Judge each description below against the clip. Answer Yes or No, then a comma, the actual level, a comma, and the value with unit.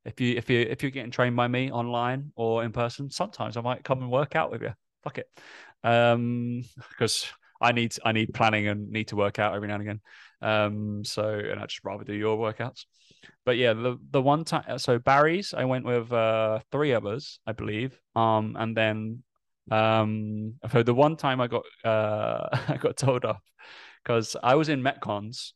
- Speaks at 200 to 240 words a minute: Yes, fast, 205 wpm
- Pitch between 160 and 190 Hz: No, low, 115 Hz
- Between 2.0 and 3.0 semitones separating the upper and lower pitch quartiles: Yes, narrow, 2.4 semitones